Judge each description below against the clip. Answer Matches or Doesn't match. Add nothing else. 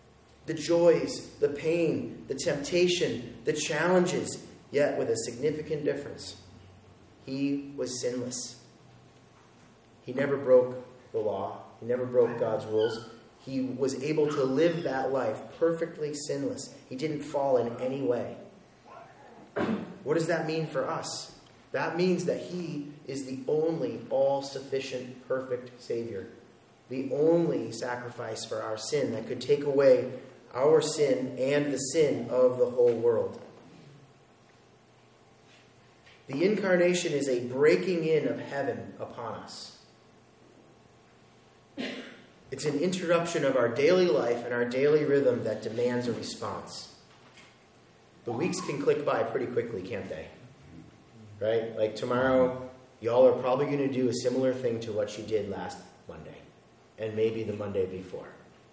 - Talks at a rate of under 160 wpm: Matches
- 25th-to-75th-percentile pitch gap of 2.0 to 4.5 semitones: Doesn't match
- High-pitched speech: Doesn't match